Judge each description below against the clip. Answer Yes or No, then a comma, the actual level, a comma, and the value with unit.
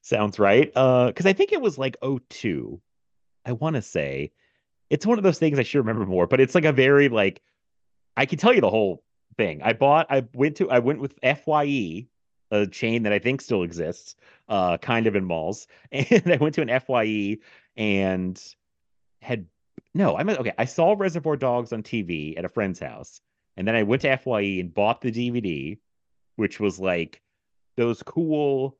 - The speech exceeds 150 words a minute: Yes, average, 200 wpm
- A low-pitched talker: Yes, low, 125 Hz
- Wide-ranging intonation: Yes, wide, 5.8 semitones